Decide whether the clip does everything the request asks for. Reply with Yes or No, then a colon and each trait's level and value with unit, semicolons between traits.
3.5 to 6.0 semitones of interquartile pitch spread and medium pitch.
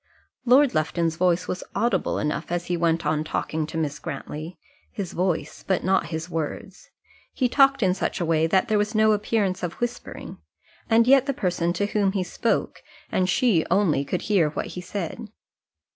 Yes: average, 4.4 semitones; medium, 180 Hz